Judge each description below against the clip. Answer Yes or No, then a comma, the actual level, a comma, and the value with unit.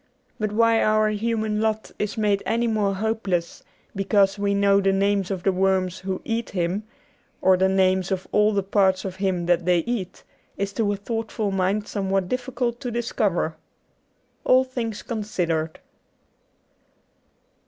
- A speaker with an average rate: Yes, average, 155 wpm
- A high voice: Yes, high, 200 Hz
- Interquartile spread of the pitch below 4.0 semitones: Yes, narrow, 2.5 semitones